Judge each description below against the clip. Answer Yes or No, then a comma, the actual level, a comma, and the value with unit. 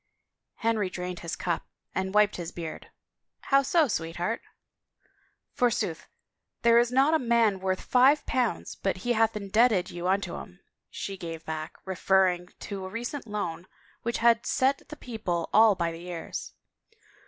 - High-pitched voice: Yes, high, 205 Hz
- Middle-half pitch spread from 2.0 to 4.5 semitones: No, average, 4.9 semitones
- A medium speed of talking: Yes, average, 160 wpm